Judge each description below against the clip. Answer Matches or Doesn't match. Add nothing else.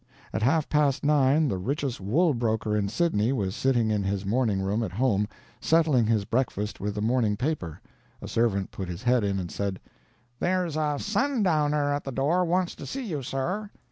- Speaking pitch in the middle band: Doesn't match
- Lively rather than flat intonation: Matches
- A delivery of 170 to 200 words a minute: Matches